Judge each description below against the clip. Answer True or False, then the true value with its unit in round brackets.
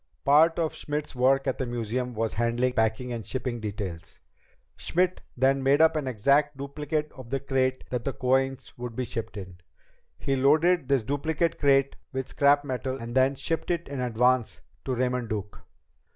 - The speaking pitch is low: True (130 Hz)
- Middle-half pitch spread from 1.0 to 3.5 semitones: True (2.8 semitones)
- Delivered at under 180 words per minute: True (170 wpm)